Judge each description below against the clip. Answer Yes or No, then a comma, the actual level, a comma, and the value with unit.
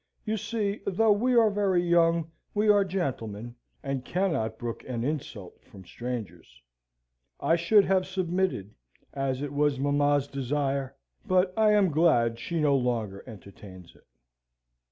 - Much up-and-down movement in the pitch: Yes, wide, 7.8 semitones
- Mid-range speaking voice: Yes, medium, 145 Hz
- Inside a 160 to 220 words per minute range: No, average, 140 wpm